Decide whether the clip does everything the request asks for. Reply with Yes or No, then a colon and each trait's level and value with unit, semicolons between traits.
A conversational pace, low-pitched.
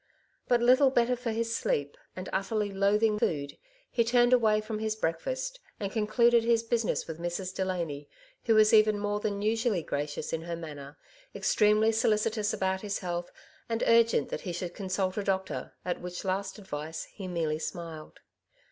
No: average, 175 wpm; high, 205 Hz